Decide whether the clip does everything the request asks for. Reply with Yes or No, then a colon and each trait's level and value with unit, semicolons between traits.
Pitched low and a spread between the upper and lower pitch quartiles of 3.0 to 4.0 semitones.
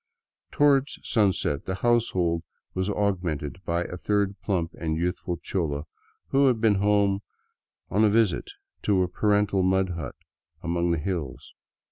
Yes: very low, 95 Hz; average, 3.3 semitones